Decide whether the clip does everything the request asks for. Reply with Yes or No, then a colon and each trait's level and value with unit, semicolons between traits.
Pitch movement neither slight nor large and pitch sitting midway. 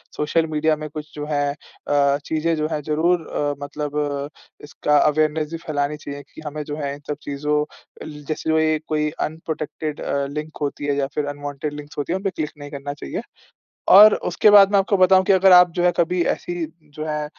No: narrow, 1.9 semitones; medium, 150 Hz